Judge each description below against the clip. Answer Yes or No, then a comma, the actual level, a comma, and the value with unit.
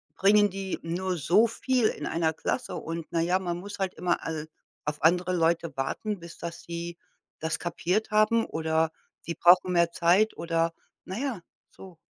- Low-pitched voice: No, medium, 175 Hz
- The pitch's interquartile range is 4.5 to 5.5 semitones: No, average, 2.8 semitones